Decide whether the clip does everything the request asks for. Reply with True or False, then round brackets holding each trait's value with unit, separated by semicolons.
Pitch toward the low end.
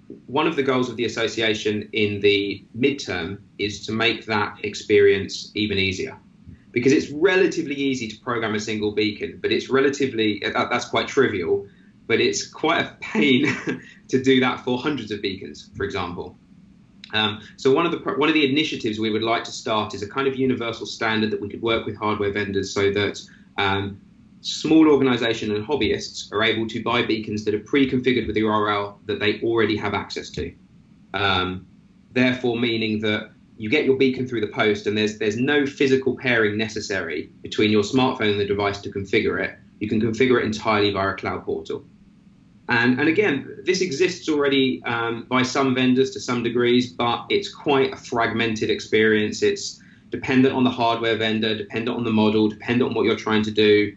True (115 Hz)